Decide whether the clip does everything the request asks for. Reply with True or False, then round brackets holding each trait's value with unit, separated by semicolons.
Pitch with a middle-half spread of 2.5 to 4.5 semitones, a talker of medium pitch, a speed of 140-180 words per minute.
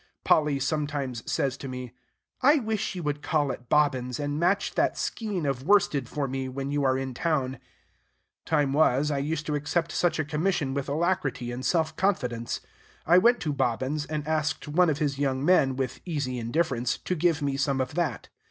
False (3.3 semitones; 145 Hz; 190 wpm)